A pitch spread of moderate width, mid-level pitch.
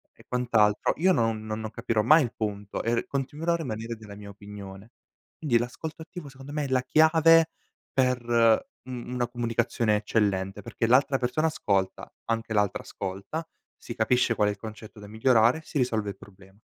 No: average, 4.2 semitones; low, 115 Hz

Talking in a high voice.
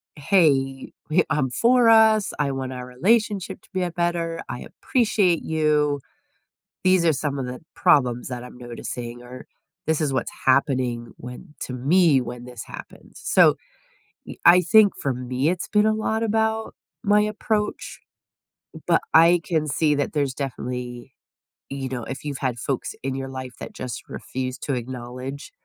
No: medium, 140 Hz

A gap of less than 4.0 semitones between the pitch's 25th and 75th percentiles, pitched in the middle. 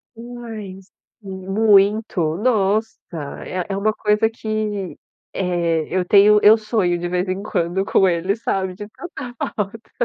No: average, 2.7 semitones; high, 200 Hz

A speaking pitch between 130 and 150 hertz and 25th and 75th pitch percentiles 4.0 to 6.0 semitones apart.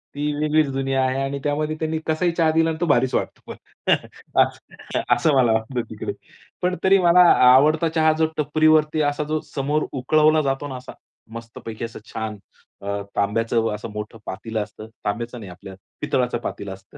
Yes: low, 135 Hz; wide, 5.4 semitones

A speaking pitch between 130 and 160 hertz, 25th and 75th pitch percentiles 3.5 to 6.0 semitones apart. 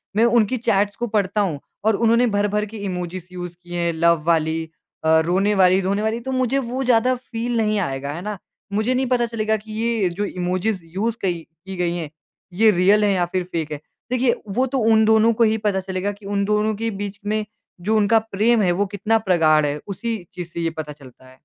No: high, 205 Hz; average, 3.9 semitones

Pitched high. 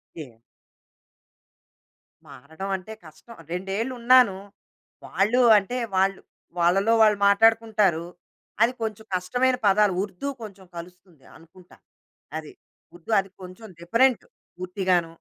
Yes: high, 195 Hz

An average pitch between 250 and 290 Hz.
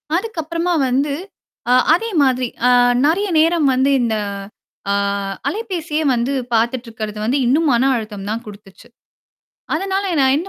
Yes: very high, 270 Hz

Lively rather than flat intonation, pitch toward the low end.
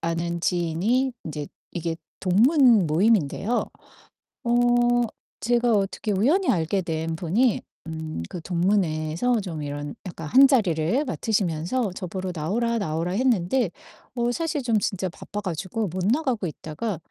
No: wide, 6.2 semitones; high, 190 Hz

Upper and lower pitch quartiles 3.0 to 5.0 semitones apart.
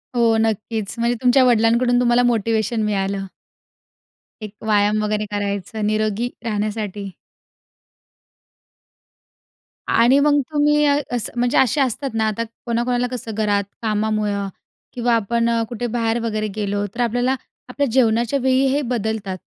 No: narrow, 2.5 semitones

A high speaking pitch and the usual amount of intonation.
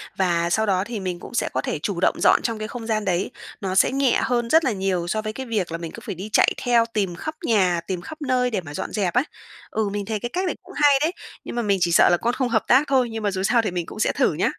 Yes: high, 215 Hz; average, 4.6 semitones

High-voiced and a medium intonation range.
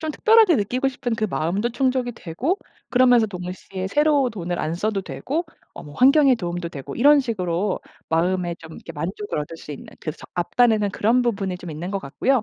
No: high, 205 Hz; wide, 6.5 semitones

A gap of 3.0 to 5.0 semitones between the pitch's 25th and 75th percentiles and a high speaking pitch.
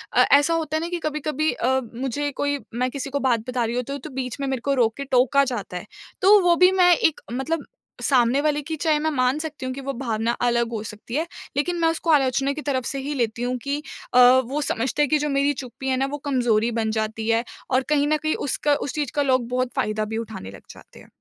Yes: average, 3.4 semitones; very high, 270 Hz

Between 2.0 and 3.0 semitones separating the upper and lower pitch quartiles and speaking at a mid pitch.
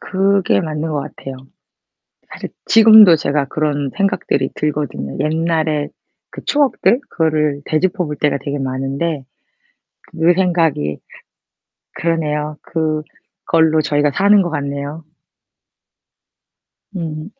Yes: average, 2.7 semitones; medium, 155 Hz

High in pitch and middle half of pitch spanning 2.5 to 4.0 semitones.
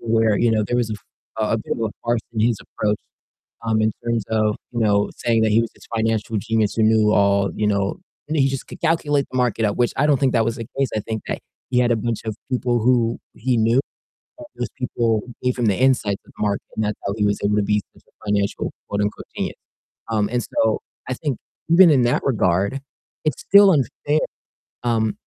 No: low, 115 Hz; average, 2.8 semitones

